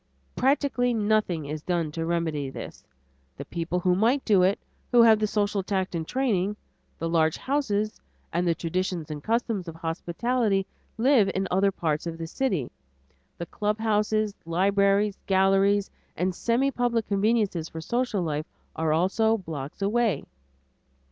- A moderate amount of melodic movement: Yes, average, 4.6 semitones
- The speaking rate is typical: Yes, average, 150 wpm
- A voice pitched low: No, high, 195 Hz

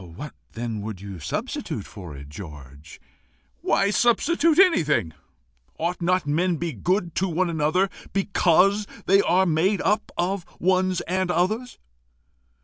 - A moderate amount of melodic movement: No, wide, 9.0 semitones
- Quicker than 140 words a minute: No, slow, 135 wpm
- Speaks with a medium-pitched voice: Yes, medium, 175 Hz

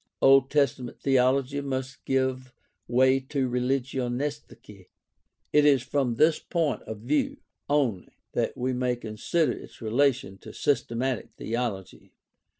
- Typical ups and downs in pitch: No, narrow, 2.3 semitones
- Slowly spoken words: Yes, slow, 120 wpm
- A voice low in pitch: Yes, low, 130 Hz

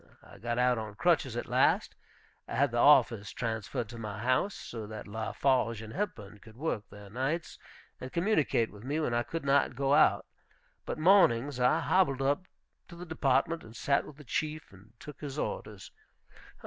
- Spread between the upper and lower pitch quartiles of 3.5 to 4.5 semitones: No, average, 5.1 semitones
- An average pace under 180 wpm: No, average, 185 wpm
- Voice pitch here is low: Yes, low, 130 Hz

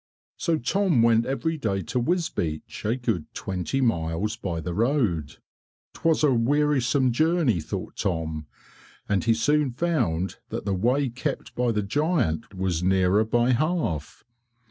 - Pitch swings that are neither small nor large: No, wide, 7.5 semitones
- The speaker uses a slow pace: No, average, 145 wpm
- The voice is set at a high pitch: No, low, 115 Hz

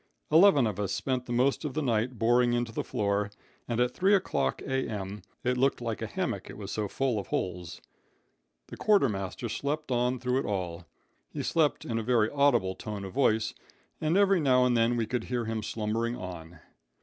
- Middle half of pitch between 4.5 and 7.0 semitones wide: No, average, 4.0 semitones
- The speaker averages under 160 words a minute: No, average, 195 wpm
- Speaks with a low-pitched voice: Yes, low, 120 Hz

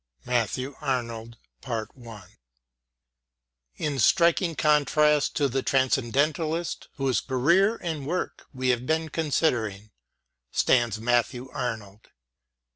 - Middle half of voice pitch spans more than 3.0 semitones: Yes, average, 4.3 semitones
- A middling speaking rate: No, slow, 90 wpm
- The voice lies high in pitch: No, low, 135 Hz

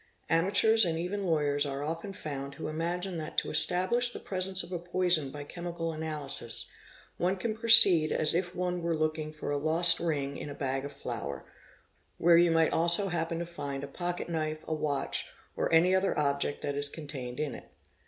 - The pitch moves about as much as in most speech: Yes, average, 3.5 semitones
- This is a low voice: No, medium, 165 Hz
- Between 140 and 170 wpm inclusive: No, average, 200 wpm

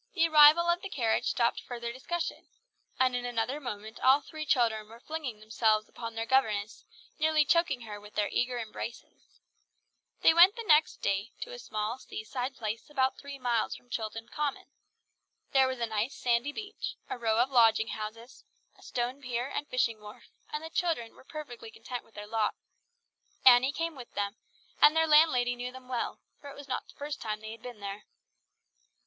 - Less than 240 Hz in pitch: No, high, 245 Hz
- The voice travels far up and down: No, average, 4.6 semitones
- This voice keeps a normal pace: Yes, average, 190 wpm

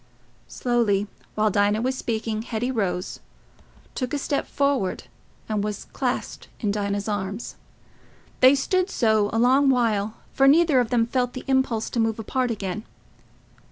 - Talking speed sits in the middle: Yes, average, 150 wpm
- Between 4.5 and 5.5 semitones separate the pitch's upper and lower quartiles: No, average, 3.7 semitones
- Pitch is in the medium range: No, high, 230 Hz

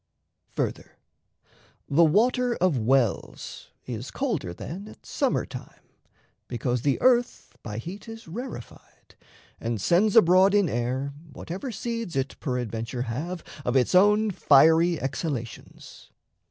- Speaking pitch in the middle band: Yes, medium, 160 Hz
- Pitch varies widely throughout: Yes, wide, 8.7 semitones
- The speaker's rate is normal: No, slow, 120 wpm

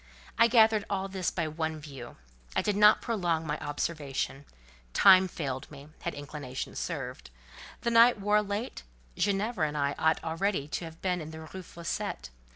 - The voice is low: No, medium, 165 Hz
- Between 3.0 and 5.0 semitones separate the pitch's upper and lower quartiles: No, wide, 5.6 semitones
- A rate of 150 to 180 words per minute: Yes, average, 160 wpm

